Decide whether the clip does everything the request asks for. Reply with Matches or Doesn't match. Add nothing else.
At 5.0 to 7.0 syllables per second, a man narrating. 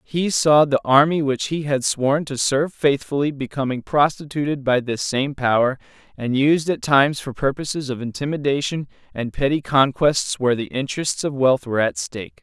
Matches